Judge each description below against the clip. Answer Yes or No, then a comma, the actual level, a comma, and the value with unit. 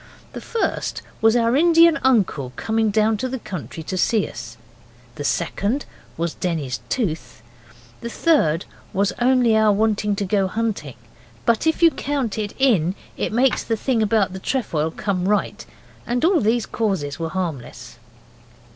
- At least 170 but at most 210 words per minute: No, average, 155 wpm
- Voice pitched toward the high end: Yes, high, 215 Hz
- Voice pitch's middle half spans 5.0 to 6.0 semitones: Yes, wide, 5.6 semitones